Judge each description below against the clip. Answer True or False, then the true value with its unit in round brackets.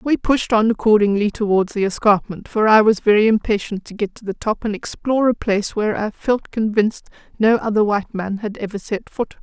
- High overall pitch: True (215 Hz)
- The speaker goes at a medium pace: False (210 wpm)